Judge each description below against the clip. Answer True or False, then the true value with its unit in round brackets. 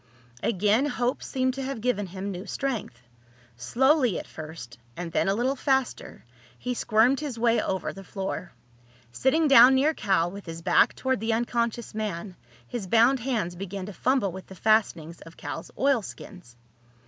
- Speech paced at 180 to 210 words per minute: False (165 wpm)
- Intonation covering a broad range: True (5.8 semitones)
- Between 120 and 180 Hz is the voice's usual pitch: False (215 Hz)